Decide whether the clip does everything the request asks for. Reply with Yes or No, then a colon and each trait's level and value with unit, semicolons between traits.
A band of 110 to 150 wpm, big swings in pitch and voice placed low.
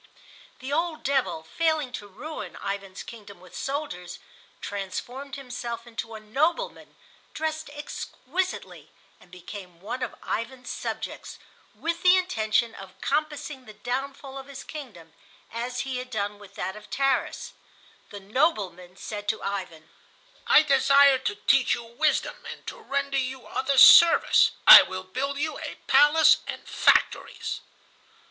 No: average, 140 wpm; wide, 5.7 semitones; very high, 250 Hz